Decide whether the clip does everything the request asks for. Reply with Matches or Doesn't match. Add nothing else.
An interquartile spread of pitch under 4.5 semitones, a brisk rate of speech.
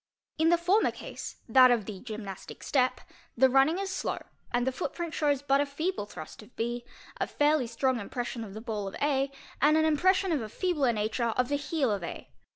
Doesn't match